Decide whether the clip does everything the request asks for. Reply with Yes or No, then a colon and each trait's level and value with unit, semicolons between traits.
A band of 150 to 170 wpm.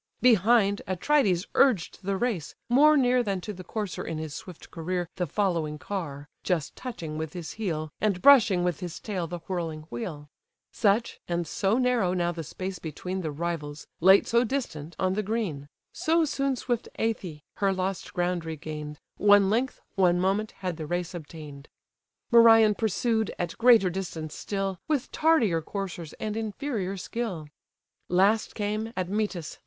Yes: average, 160 wpm